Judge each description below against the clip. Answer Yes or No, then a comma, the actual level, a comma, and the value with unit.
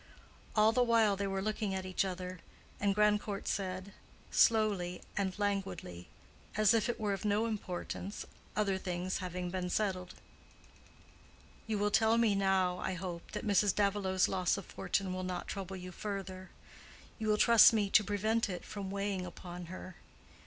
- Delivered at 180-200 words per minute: No, average, 165 wpm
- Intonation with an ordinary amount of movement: No, narrow, 2.3 semitones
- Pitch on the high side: Yes, high, 195 Hz